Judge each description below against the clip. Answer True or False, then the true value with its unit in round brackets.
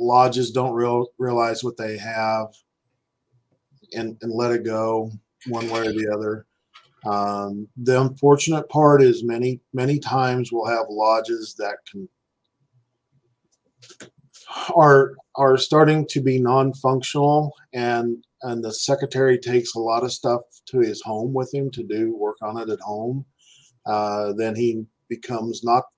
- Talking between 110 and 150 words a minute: True (145 wpm)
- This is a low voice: True (120 Hz)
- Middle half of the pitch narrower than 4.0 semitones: True (2.8 semitones)